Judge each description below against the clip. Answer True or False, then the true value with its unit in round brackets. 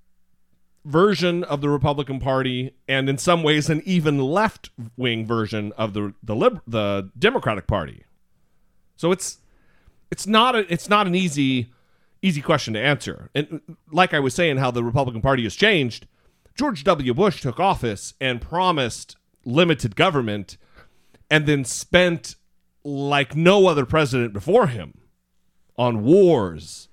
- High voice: False (140 Hz)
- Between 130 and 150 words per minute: True (145 wpm)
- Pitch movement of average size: False (6.7 semitones)